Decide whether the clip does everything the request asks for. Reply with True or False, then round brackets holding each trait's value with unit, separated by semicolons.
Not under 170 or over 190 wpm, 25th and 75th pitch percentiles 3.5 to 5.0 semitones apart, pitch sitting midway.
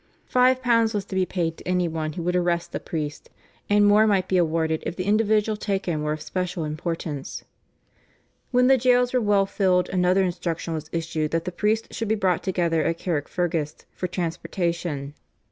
True (185 wpm; 3.9 semitones; 180 Hz)